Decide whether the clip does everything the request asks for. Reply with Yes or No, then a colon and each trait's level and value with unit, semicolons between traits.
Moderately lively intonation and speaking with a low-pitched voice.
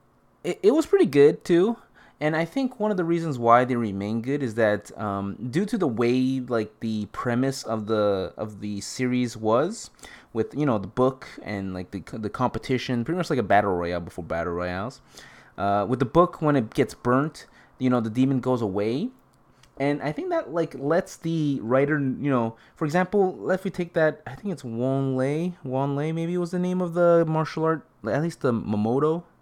No: wide, 6.3 semitones; low, 130 Hz